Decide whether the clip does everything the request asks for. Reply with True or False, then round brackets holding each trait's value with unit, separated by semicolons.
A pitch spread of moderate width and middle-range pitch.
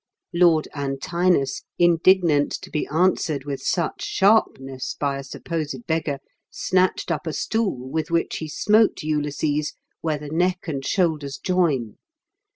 True (3.8 semitones; 155 Hz)